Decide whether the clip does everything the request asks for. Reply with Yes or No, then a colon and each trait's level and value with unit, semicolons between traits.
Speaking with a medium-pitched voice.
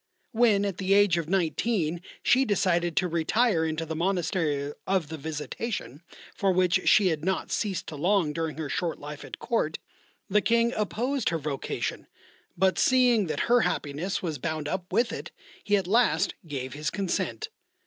Yes: medium, 180 Hz